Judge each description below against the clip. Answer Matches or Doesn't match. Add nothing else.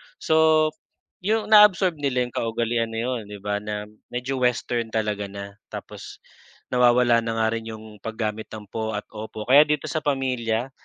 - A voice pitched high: Doesn't match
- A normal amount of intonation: Matches